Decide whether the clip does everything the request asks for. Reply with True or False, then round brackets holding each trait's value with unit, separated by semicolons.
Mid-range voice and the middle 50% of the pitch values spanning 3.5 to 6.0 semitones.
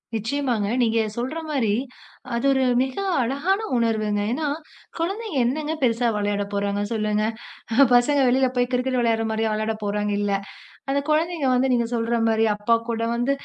False (235 Hz; 3.8 semitones)